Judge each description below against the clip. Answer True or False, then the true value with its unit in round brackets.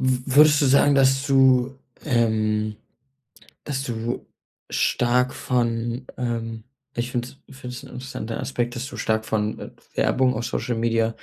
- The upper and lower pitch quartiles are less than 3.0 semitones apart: True (2.5 semitones)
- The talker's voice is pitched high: False (125 Hz)